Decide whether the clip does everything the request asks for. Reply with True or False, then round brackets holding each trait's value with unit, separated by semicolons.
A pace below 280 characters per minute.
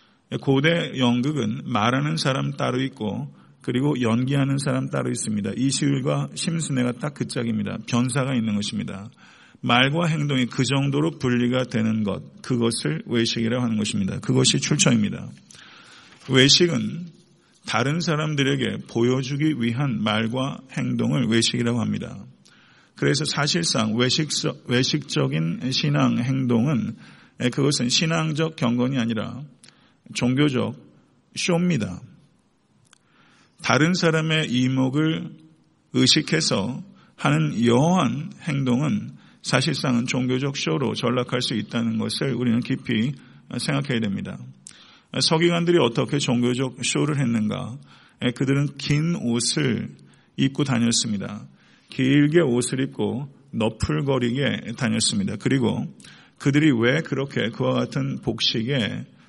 True (265 characters per minute)